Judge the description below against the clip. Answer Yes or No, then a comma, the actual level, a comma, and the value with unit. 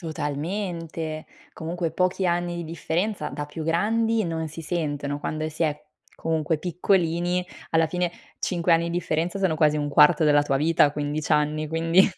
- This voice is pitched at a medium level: Yes, medium, 165 Hz